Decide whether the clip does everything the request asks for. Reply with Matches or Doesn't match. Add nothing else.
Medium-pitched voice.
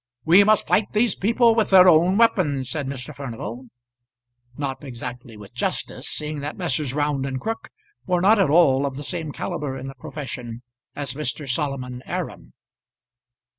Matches